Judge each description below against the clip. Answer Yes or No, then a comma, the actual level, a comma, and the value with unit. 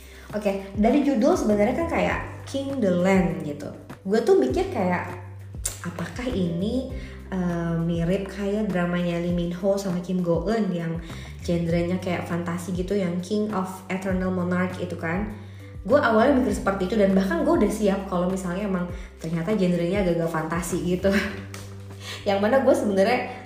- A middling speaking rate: No, fast, 160 wpm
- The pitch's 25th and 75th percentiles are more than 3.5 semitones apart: No, average, 3.0 semitones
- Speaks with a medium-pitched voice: Yes, medium, 180 Hz